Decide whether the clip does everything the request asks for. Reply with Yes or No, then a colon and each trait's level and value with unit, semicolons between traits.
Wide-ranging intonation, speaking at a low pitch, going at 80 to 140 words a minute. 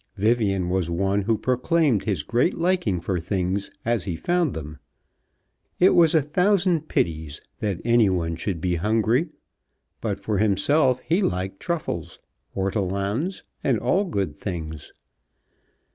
Yes: wide, 8.3 semitones; low, 100 Hz; slow, 135 wpm